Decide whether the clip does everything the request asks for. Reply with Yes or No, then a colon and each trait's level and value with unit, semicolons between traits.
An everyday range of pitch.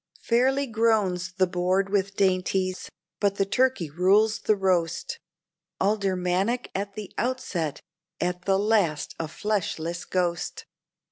Yes: average, 3.1 semitones